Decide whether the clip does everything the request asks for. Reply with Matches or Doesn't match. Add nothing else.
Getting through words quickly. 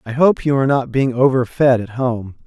Matches